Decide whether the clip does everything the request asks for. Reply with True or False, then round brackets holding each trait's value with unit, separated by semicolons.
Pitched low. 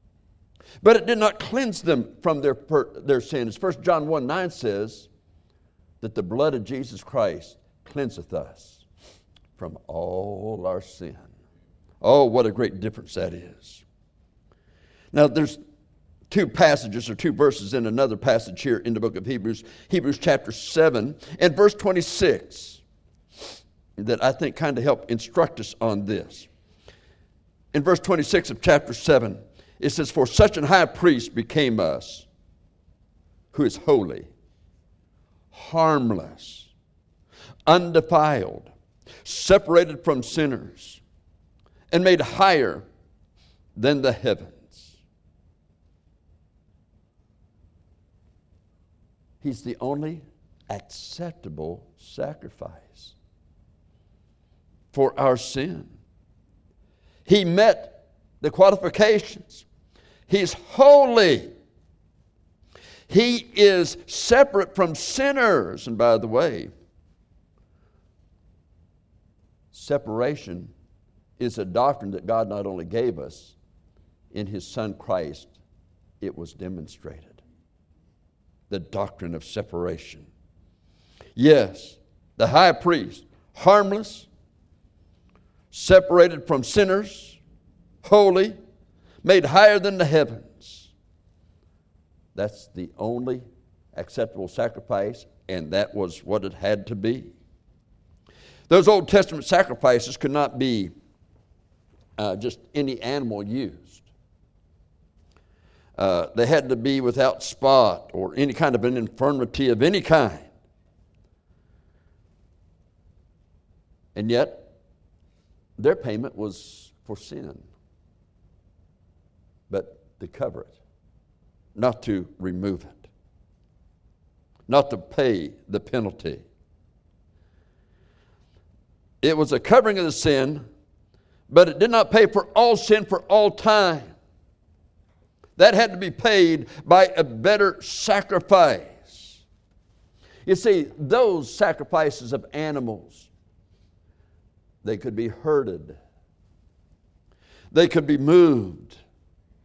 True (100 Hz)